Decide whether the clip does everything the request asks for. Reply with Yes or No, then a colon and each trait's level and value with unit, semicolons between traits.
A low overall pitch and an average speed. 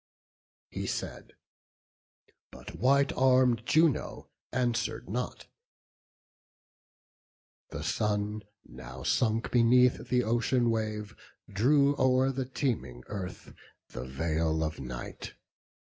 No: low, 115 Hz; slow, 95 wpm